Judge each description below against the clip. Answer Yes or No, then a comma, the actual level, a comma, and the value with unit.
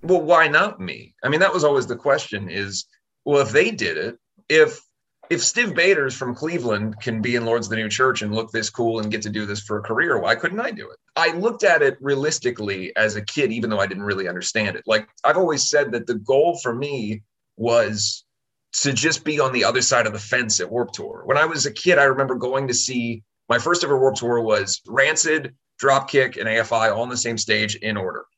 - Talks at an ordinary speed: No, fast, 240 wpm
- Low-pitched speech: Yes, low, 120 Hz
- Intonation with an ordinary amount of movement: Yes, average, 3.9 semitones